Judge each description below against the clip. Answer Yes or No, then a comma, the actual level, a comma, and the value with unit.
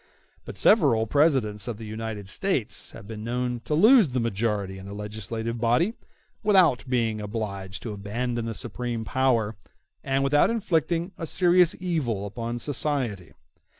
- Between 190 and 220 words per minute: No, average, 150 wpm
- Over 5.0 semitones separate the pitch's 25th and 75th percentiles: Yes, wide, 5.5 semitones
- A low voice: Yes, low, 120 Hz